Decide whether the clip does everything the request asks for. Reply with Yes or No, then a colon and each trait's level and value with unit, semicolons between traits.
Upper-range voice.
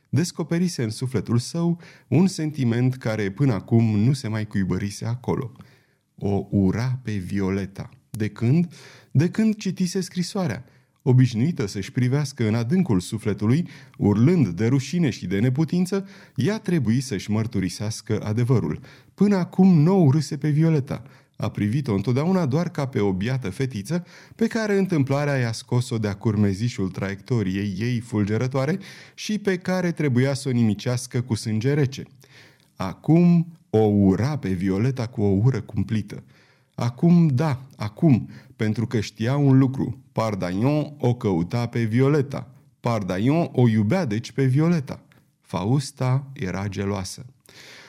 No: low, 130 Hz